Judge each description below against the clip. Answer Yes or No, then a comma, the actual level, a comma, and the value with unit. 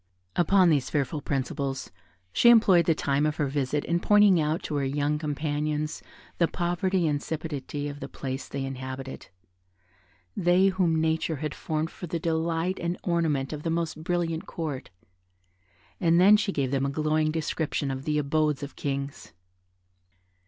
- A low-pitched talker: No, medium, 155 Hz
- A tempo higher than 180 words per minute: No, average, 160 wpm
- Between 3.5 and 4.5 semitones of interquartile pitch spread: No, average, 3.1 semitones